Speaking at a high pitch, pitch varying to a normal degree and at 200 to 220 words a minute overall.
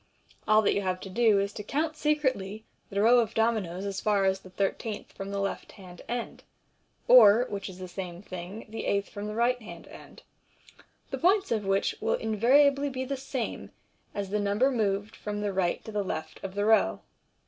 Yes: high, 210 Hz; average, 3.3 semitones; fast, 205 wpm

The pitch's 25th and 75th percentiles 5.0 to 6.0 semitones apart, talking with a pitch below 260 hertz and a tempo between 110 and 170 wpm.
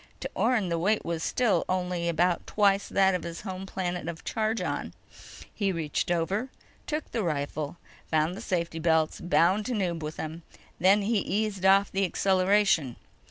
No: average, 3.2 semitones; medium, 185 Hz; average, 160 wpm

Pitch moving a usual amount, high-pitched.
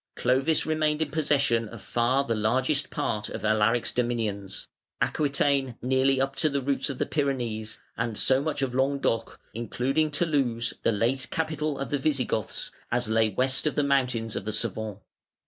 No: average, 3.6 semitones; low, 130 Hz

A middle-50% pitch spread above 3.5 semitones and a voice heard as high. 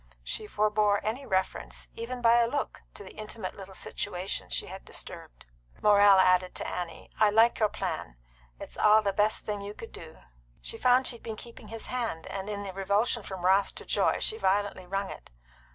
No: average, 2.9 semitones; high, 205 Hz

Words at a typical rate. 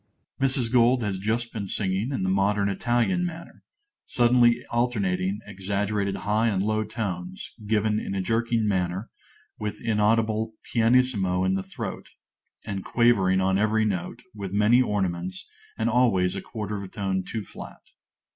Yes: average, 155 wpm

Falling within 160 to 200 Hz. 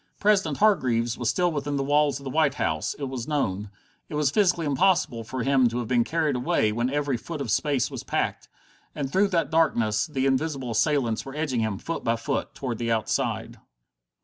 No: low, 135 Hz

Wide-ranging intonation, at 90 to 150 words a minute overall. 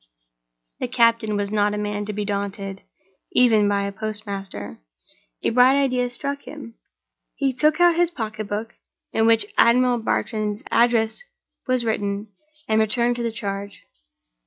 No: average, 3.2 semitones; average, 145 wpm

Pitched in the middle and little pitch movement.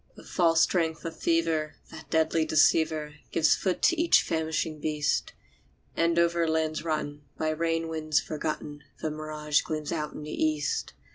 Yes: medium, 155 Hz; narrow, 1.2 semitones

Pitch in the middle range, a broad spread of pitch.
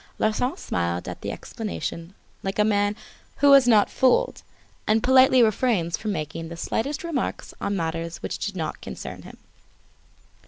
No: high, 205 Hz; wide, 7.0 semitones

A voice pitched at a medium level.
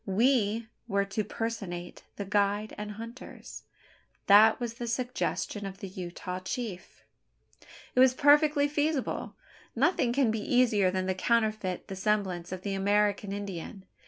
No: high, 210 Hz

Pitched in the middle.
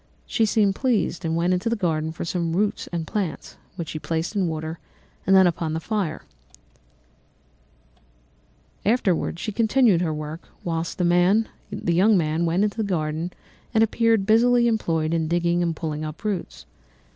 Yes: medium, 175 Hz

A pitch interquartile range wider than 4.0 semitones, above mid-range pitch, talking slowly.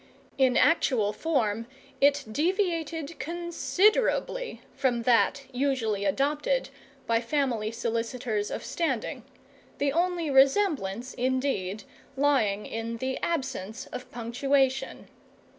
Yes: average, 4.7 semitones; very high, 265 Hz; slow, 95 wpm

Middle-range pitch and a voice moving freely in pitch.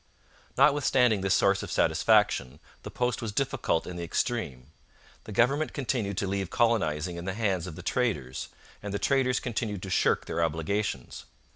No: low, 100 Hz; wide, 6.0 semitones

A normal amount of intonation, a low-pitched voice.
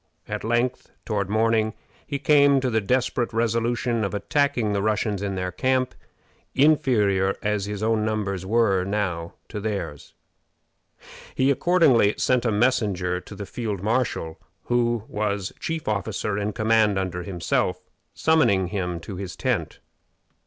Yes: average, 3.6 semitones; low, 105 Hz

